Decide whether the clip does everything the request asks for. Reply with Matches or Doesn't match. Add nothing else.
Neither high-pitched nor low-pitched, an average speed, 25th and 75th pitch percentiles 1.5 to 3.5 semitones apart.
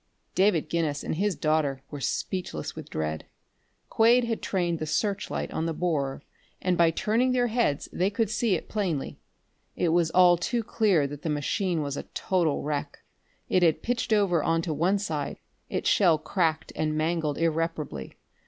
Doesn't match